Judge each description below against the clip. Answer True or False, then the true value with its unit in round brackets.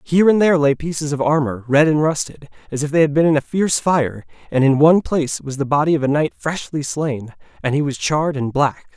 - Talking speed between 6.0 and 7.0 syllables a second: True (6.1 syllables/s)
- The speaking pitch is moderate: True (150 Hz)